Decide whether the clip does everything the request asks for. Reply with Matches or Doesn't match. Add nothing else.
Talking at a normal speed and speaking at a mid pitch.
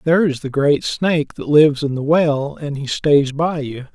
Doesn't match